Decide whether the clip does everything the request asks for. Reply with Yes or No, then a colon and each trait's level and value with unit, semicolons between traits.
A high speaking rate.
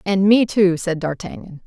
No: average, 180 wpm